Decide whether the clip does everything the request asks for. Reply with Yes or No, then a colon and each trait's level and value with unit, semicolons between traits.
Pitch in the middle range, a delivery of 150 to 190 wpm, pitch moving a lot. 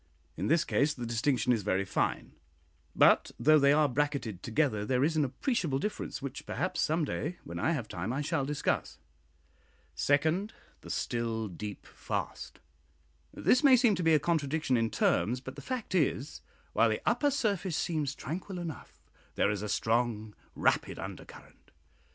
Yes: medium, 145 Hz; average, 165 wpm; wide, 6.0 semitones